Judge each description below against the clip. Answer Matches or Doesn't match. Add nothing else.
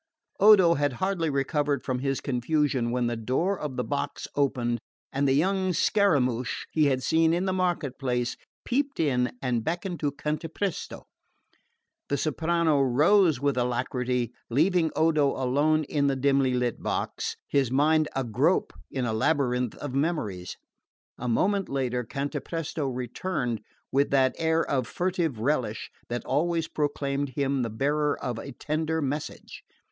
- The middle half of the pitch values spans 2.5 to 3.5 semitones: Doesn't match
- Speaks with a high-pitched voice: Doesn't match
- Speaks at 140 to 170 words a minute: Matches